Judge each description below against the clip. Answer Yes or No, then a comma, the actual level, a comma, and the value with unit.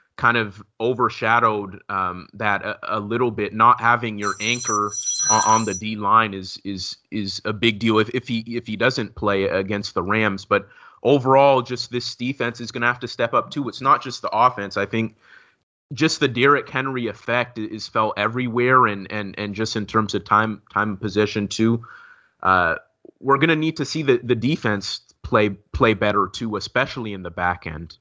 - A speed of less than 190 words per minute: No, average, 200 wpm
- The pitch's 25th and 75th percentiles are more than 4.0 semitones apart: No, average, 3.0 semitones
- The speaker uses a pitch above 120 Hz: No, low, 110 Hz